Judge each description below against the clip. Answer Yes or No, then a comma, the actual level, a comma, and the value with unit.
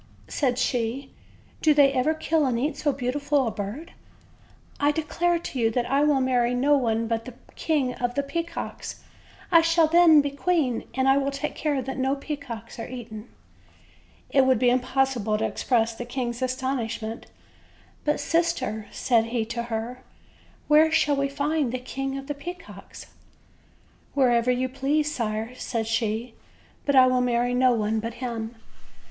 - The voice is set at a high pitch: Yes, very high, 260 Hz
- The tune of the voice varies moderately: Yes, average, 3.4 semitones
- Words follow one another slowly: No, average, 170 wpm